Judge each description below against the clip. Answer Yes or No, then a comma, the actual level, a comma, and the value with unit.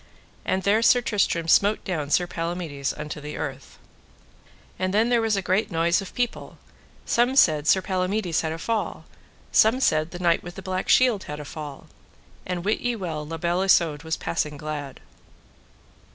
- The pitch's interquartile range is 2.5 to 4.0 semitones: No, average, 4.6 semitones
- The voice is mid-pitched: Yes, medium, 175 Hz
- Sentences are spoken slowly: No, average, 180 wpm